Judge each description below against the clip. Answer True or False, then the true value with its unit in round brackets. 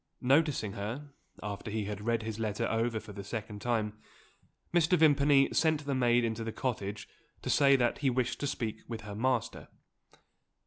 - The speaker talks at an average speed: True (175 wpm)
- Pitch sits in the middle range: False (115 Hz)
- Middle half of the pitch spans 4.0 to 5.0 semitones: True (4.3 semitones)